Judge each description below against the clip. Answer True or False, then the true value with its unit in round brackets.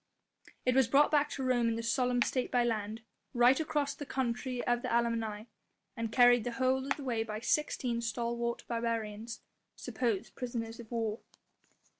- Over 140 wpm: True (165 wpm)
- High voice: True (235 Hz)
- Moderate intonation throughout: False (2.0 semitones)